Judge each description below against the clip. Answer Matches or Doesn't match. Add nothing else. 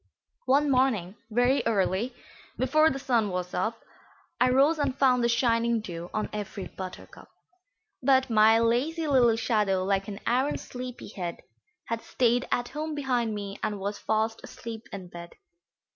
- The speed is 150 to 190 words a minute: Matches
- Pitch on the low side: Doesn't match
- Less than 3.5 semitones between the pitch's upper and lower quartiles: Doesn't match